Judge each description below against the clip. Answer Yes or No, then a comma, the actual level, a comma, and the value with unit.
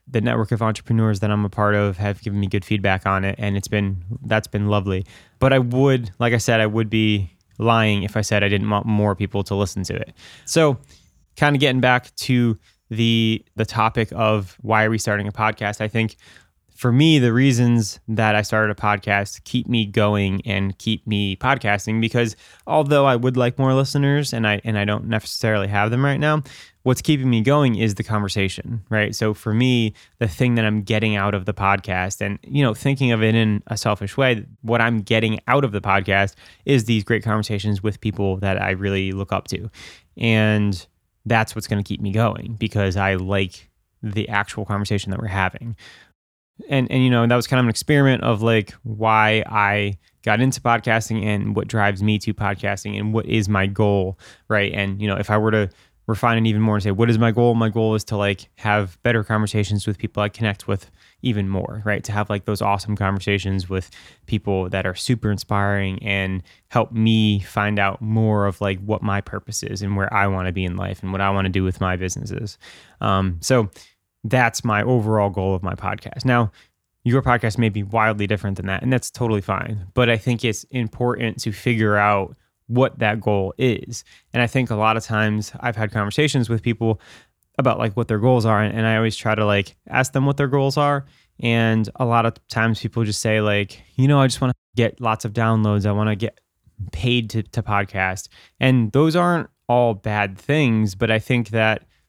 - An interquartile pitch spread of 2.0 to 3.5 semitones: Yes, narrow, 2.5 semitones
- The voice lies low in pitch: Yes, low, 110 Hz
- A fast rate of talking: Yes, fast, 215 wpm